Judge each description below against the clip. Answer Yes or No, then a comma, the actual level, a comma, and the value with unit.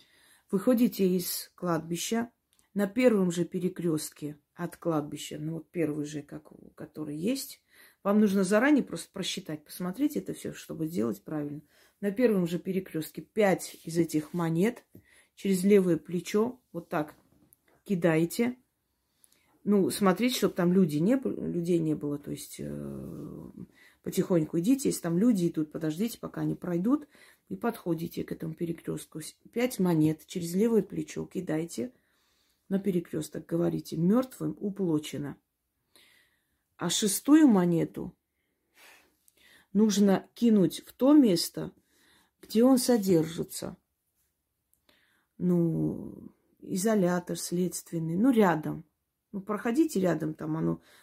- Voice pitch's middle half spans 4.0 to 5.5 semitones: Yes, average, 4.7 semitones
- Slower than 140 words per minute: Yes, average, 120 wpm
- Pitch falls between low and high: Yes, medium, 175 Hz